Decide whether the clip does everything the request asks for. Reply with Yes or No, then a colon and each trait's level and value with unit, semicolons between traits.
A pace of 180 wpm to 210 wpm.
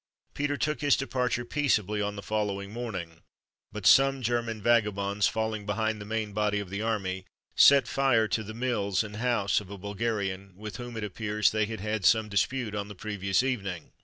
Yes: average, 190 wpm